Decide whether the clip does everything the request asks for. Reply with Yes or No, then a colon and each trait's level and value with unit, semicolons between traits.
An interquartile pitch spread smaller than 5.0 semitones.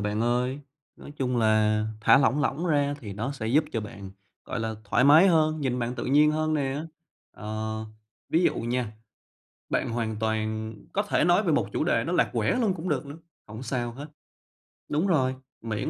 No: average, 5.3 semitones